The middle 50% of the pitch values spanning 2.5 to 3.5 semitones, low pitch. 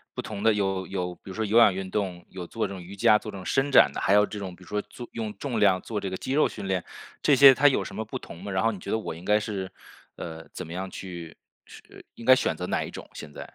Yes: average, 2.9 semitones; low, 100 Hz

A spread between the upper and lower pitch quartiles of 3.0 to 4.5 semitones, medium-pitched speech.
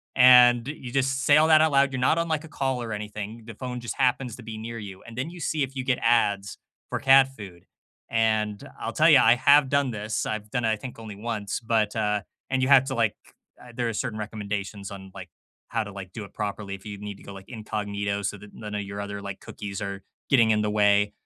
No: average, 3.9 semitones; low, 110 Hz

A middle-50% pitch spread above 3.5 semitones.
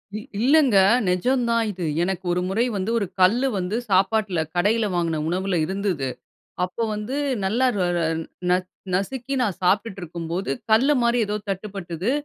Yes: average, 4.3 semitones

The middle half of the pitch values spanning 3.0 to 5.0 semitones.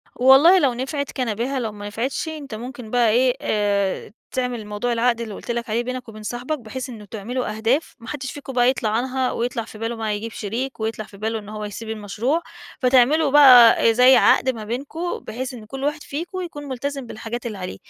Yes: average, 3.3 semitones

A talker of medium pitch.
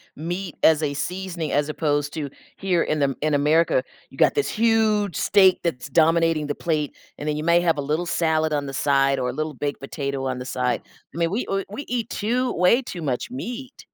Yes: medium, 160 Hz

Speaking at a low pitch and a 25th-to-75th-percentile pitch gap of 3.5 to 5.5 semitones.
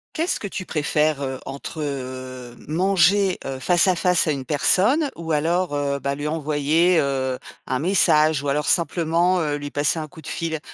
No: medium, 155 Hz; average, 3.8 semitones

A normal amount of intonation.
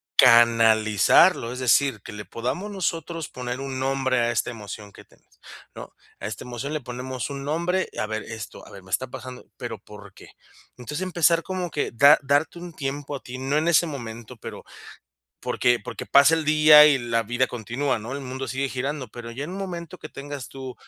Yes: average, 4.2 semitones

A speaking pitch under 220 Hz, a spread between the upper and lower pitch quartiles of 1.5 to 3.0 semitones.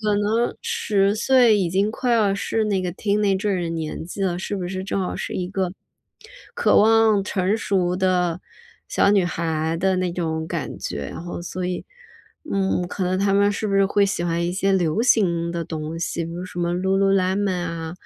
Yes: high, 190 Hz; narrow, 2.6 semitones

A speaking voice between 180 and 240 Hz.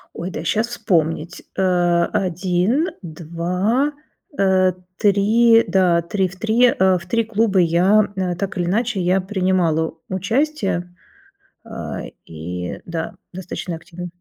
Yes: medium, 185 Hz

